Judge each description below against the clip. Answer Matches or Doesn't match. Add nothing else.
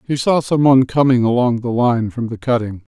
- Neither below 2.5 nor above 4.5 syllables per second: Doesn't match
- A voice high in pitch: Doesn't match